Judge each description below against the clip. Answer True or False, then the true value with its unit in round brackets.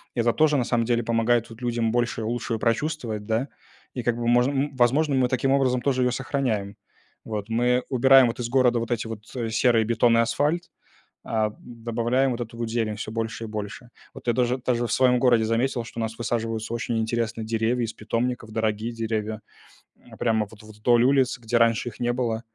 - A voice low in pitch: True (120 Hz)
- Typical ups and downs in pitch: False (1.7 semitones)